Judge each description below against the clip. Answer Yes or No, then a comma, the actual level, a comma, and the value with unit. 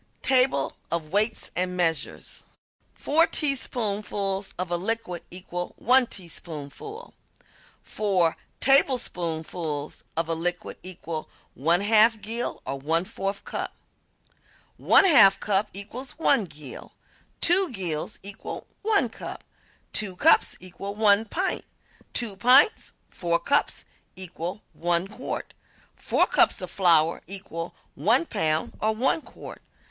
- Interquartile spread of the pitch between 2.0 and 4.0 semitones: No, average, 5.1 semitones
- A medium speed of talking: No, slow, 115 wpm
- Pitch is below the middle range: No, high, 195 Hz